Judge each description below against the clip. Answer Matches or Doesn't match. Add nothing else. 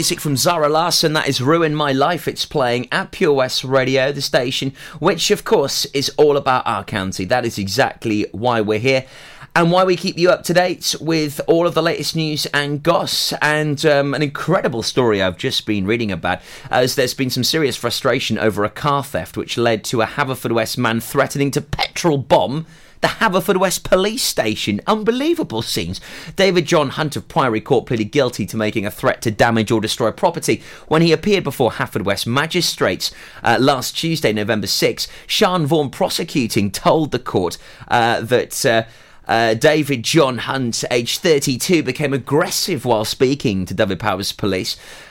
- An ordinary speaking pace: Matches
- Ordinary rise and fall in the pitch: Doesn't match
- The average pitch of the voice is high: Doesn't match